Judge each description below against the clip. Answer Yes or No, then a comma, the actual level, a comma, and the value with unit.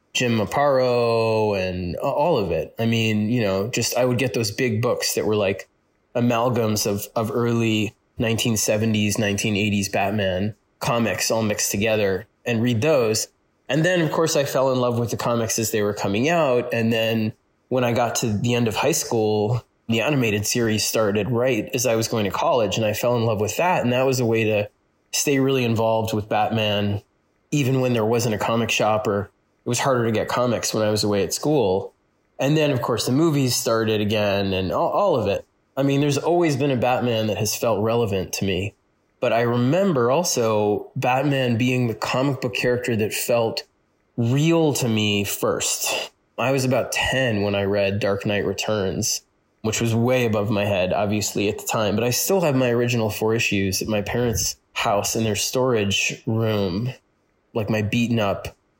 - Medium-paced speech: Yes, average, 195 wpm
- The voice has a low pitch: Yes, low, 115 Hz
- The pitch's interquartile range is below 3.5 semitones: Yes, average, 2.9 semitones